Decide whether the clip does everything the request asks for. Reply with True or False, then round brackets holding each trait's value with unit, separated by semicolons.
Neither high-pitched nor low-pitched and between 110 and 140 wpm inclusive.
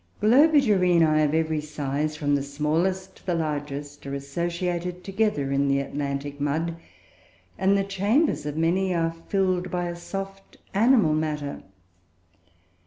True (165 Hz; 135 wpm)